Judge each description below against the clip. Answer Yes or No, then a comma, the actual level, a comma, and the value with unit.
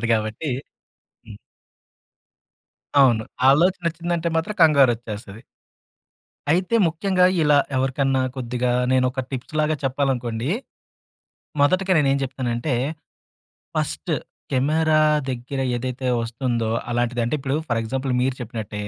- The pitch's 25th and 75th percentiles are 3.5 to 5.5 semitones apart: Yes, average, 4.2 semitones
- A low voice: Yes, low, 130 Hz